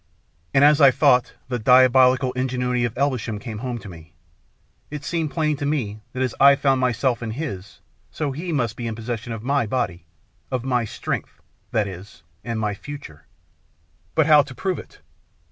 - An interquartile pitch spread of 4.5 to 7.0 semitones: No, average, 3.8 semitones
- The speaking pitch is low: Yes, low, 125 Hz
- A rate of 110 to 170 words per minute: No, average, 180 wpm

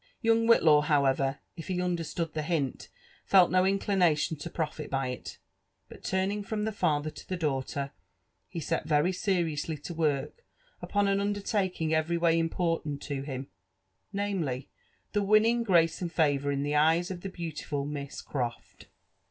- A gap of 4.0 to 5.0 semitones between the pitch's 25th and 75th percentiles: Yes, average, 4.3 semitones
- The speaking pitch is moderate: Yes, medium, 165 Hz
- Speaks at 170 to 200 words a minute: No, average, 160 wpm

